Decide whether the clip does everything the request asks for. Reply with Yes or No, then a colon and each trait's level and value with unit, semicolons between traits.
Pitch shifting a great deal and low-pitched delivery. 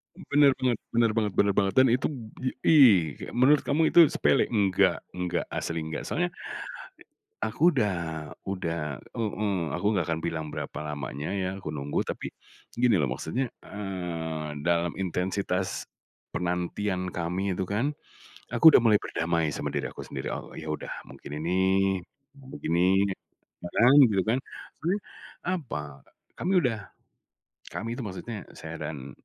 Yes: wide, 6.0 semitones; very low, 95 Hz